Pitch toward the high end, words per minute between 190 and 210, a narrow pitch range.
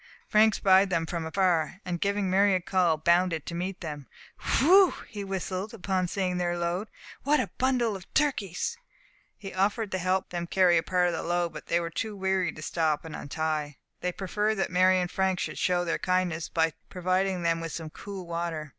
No: medium, 180 Hz; average, 200 wpm; narrow, 2.3 semitones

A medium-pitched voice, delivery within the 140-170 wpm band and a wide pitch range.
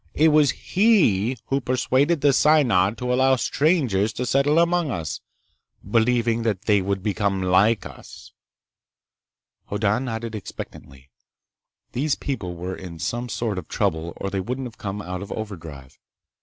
No: low, 115 Hz; average, 145 wpm; wide, 5.7 semitones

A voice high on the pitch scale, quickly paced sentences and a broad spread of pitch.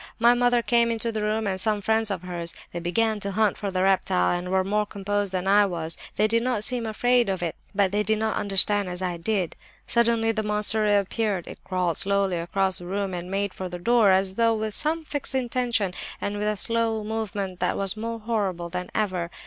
No: high, 205 Hz; fast, 230 wpm; average, 3.0 semitones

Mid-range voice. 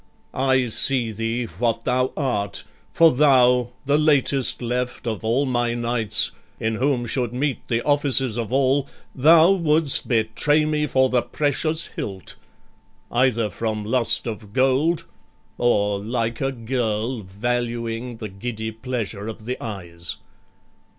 No: low, 120 Hz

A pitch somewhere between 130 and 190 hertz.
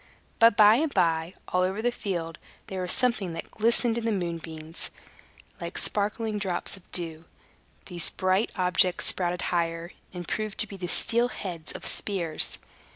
Yes: medium, 185 Hz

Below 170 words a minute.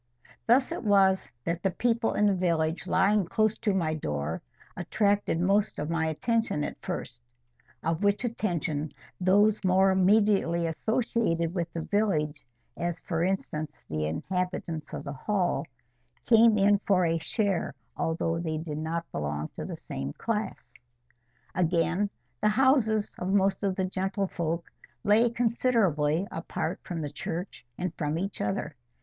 Yes: average, 145 wpm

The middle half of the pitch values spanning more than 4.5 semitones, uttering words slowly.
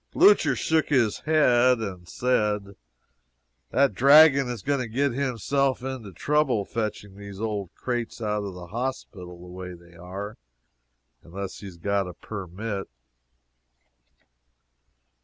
Yes: average, 5.0 semitones; slow, 130 wpm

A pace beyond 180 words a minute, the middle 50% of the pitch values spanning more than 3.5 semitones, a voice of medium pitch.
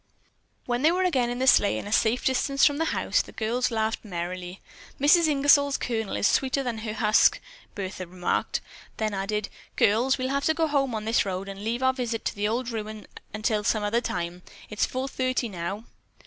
No: fast, 205 wpm; average, 4.1 semitones; high, 225 Hz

